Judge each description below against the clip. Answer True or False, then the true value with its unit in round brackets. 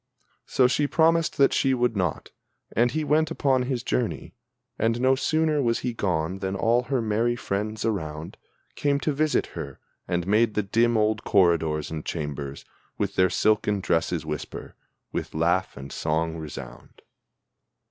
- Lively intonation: True (7.3 semitones)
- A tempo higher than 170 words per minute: False (155 wpm)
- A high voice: False (105 Hz)